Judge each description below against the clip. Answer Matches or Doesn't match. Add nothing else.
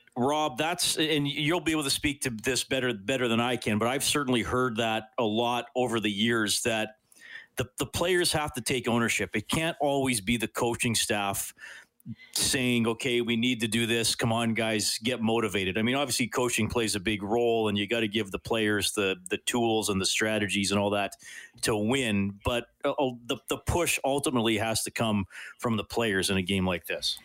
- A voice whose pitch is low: Matches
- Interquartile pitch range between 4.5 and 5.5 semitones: Doesn't match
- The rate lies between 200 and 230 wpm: Matches